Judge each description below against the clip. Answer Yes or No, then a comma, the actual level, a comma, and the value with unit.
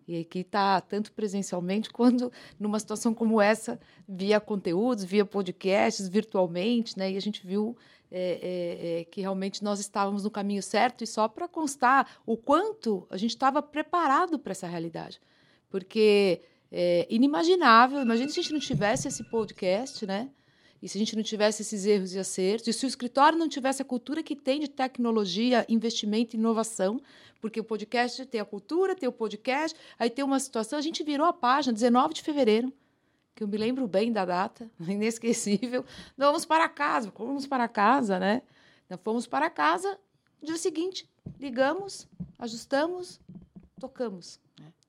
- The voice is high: Yes, high, 225 Hz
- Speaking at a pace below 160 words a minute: No, average, 165 wpm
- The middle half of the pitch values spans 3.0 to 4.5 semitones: No, average, 5.0 semitones